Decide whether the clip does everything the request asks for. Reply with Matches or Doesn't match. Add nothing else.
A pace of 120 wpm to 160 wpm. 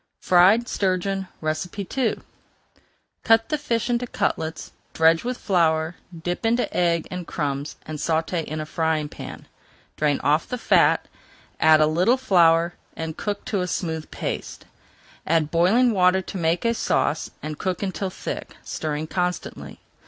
Matches